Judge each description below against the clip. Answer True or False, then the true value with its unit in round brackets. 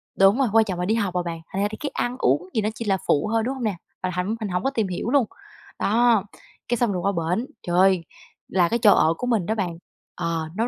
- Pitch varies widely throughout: False (4.2 semitones)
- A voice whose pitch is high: True (200 Hz)